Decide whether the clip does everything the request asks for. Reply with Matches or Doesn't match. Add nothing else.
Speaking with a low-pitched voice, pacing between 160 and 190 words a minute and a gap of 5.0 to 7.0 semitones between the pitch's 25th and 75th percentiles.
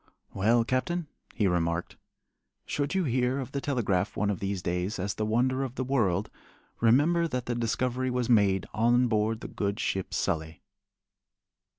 Doesn't match